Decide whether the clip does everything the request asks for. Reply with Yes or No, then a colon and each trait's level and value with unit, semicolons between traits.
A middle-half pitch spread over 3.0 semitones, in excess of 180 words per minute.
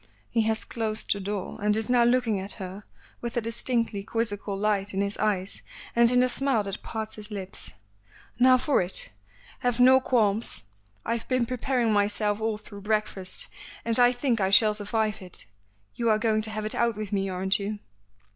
No: average, 2.7 semitones; average, 190 wpm